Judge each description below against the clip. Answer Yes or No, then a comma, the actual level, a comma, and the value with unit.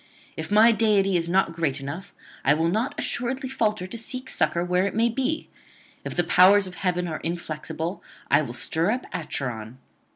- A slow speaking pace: No, average, 185 wpm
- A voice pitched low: No, medium, 180 Hz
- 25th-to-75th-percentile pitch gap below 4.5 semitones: No, average, 5.0 semitones